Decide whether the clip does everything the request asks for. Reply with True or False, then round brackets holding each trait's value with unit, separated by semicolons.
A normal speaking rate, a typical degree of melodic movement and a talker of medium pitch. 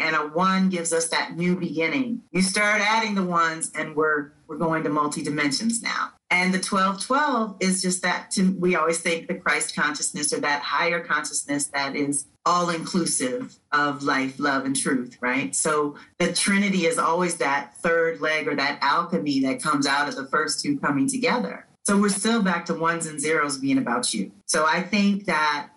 True (195 wpm; 4.1 semitones; 165 Hz)